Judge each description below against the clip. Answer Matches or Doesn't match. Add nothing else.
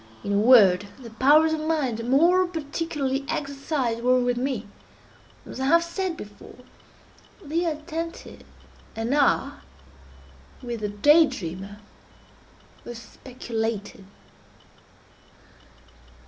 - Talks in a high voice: Matches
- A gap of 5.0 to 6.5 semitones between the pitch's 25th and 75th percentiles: Matches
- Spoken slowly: Matches